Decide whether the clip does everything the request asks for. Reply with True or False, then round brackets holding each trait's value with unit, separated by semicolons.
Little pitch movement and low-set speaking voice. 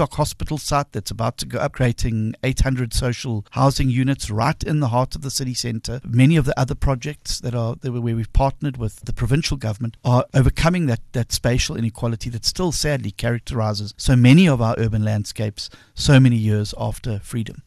False (3.4 semitones; 125 Hz)